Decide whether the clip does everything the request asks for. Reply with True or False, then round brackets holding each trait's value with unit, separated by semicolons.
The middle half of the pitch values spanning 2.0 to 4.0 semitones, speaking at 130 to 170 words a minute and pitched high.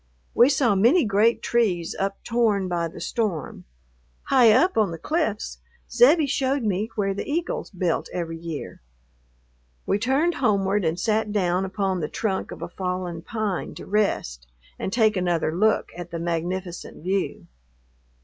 False (4.6 semitones; 150 wpm; 195 Hz)